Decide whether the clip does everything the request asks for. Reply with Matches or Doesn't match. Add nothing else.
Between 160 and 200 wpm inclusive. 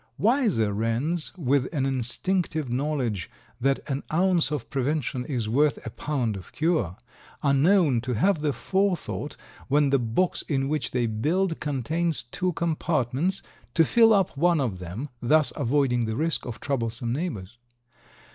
Doesn't match